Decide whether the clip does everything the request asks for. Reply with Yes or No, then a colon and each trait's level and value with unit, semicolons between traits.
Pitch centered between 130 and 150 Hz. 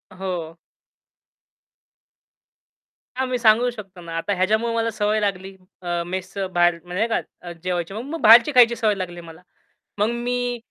No: high, 200 Hz